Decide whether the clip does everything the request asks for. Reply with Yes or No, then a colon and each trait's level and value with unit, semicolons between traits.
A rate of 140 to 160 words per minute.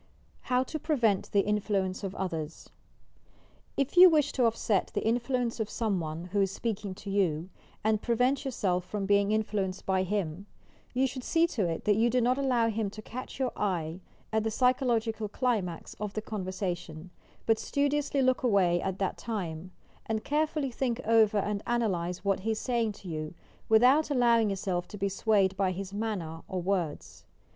No: average, 180 wpm